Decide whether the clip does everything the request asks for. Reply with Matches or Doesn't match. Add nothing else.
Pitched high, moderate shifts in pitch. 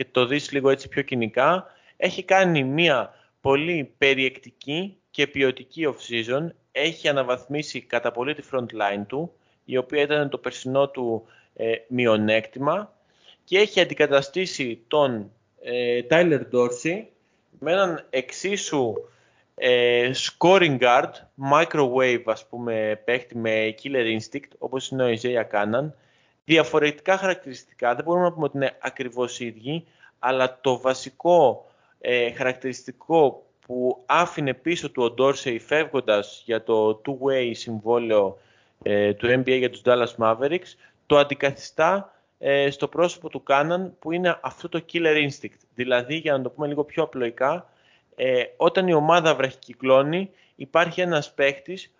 Doesn't match